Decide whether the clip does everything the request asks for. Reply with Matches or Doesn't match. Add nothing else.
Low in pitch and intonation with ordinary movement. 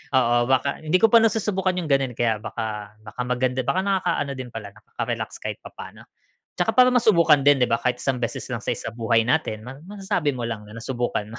Doesn't match